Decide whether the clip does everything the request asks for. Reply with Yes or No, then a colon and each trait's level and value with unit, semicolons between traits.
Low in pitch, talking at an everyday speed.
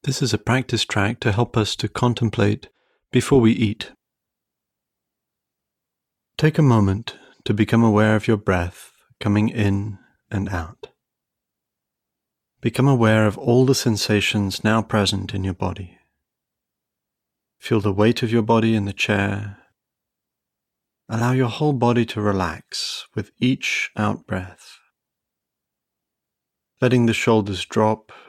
No: low, 110 Hz; slow, 125 wpm